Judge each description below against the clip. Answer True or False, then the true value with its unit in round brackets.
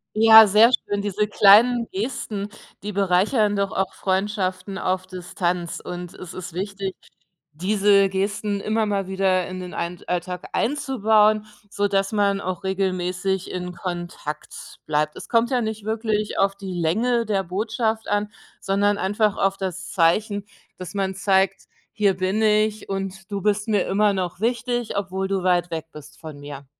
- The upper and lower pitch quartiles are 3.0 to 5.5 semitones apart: False (2.4 semitones)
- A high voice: True (195 Hz)